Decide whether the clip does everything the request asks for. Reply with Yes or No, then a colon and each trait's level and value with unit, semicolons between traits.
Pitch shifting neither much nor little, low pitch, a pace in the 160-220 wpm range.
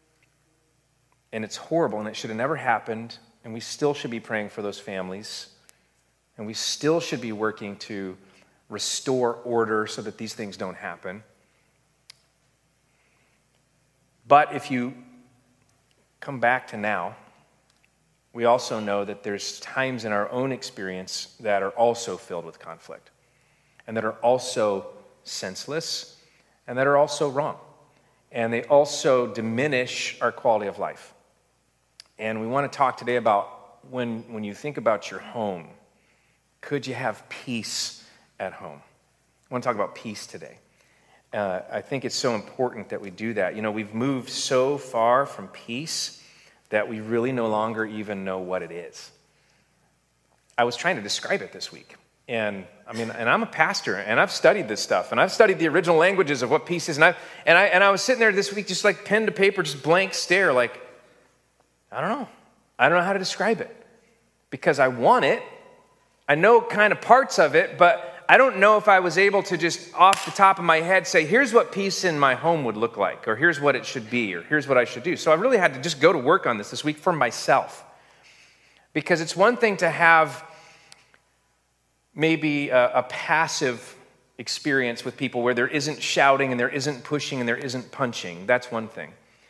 No: wide, 6.5 semitones; low, 125 Hz; average, 190 wpm